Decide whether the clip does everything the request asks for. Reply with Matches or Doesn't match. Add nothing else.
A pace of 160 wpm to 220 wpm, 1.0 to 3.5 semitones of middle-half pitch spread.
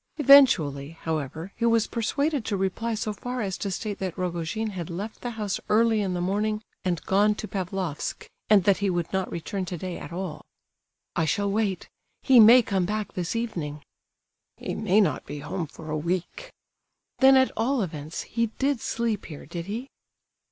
Doesn't match